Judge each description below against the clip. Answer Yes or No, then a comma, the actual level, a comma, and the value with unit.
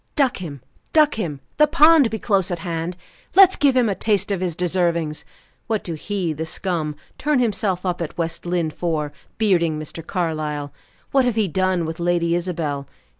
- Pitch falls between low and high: Yes, medium, 175 Hz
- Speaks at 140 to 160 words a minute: No, average, 180 wpm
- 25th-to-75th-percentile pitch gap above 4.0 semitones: Yes, average, 4.6 semitones